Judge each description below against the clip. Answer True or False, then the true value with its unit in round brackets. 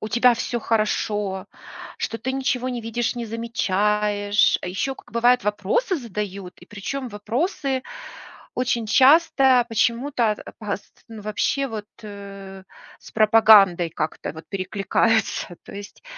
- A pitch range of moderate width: True (3.4 semitones)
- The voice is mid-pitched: False (220 Hz)